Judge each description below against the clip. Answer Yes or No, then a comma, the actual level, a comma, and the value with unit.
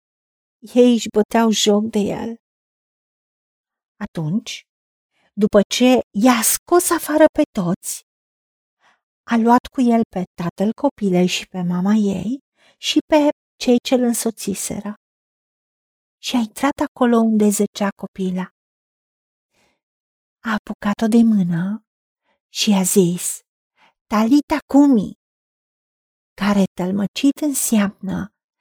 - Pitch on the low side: No, high, 220 Hz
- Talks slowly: Yes, slow, 105 wpm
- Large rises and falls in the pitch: No, average, 3.8 semitones